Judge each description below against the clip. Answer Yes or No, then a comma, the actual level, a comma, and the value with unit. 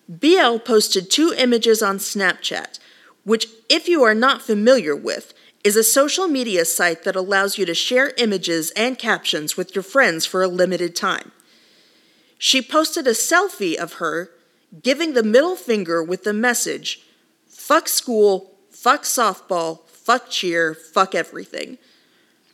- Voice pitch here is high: Yes, high, 225 Hz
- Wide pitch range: Yes, wide, 6.3 semitones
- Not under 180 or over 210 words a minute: No, average, 145 wpm